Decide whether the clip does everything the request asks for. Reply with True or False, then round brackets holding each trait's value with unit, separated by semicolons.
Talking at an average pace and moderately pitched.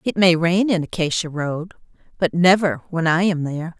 True (190 wpm; 170 Hz)